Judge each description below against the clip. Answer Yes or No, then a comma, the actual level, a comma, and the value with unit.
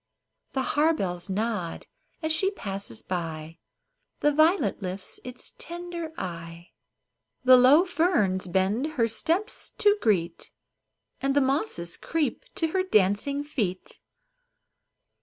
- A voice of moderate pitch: No, very high, 250 Hz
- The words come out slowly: Yes, slow, 115 wpm